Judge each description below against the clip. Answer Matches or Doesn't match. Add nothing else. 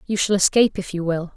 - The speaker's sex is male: Doesn't match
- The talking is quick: Matches